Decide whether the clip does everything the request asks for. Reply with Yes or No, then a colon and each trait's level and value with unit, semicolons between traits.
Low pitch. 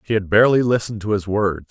Yes: low, 105 Hz